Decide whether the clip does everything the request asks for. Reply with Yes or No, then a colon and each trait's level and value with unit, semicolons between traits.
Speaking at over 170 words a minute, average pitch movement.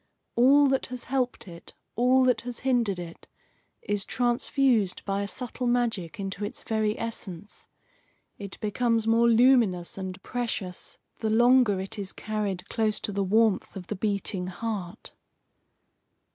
No: average, 145 wpm; average, 3.8 semitones